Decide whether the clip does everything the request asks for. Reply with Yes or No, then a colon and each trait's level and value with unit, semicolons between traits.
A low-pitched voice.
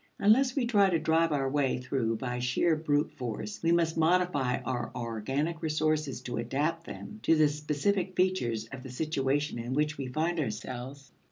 No: medium, 150 Hz